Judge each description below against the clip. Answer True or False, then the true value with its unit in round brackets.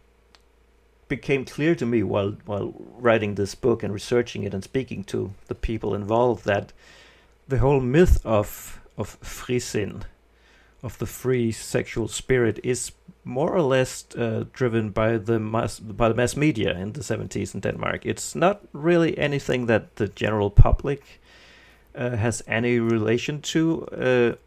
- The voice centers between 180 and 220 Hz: False (115 Hz)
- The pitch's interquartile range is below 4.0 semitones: True (3.5 semitones)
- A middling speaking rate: True (155 wpm)